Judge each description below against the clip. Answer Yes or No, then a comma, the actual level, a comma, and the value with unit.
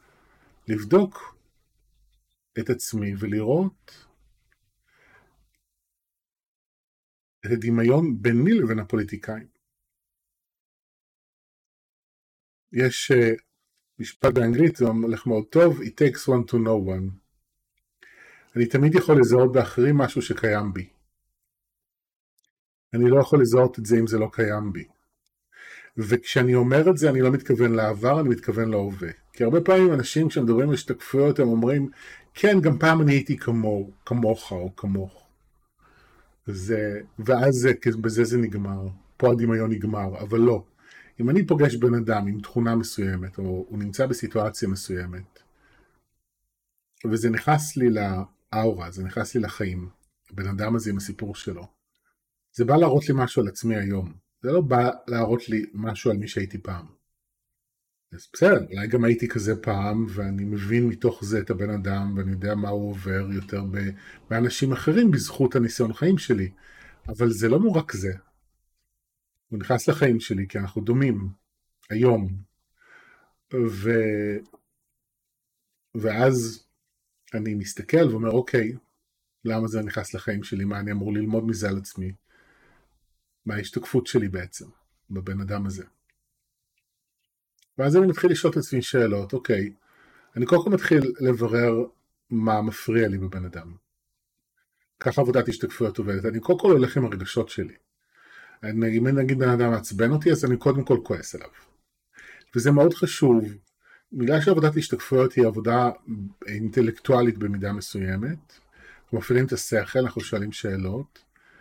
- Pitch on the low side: Yes, low, 115 Hz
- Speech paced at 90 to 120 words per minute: No, average, 135 wpm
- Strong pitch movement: No, average, 3.7 semitones